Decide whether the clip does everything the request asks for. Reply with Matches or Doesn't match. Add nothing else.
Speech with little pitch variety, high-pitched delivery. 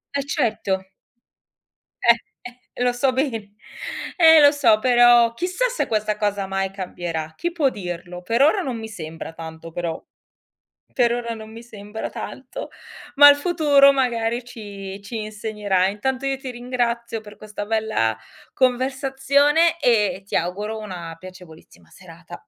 Doesn't match